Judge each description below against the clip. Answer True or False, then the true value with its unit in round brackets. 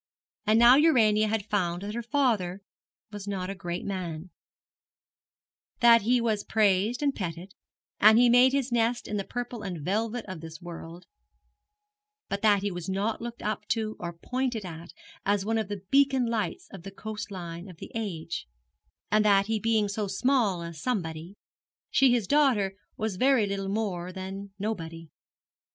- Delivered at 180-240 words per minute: False (170 wpm)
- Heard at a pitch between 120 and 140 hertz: False (205 Hz)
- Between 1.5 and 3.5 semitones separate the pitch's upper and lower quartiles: False (3.9 semitones)